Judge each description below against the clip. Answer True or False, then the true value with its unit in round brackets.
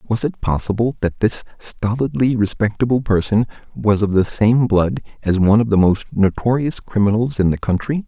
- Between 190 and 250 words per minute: False (170 wpm)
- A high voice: False (110 Hz)